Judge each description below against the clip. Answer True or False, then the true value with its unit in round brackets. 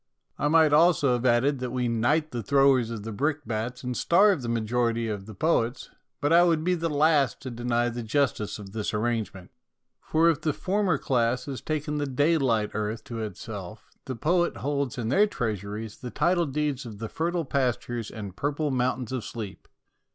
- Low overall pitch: True (130 Hz)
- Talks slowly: False (190 wpm)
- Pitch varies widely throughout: False (4.6 semitones)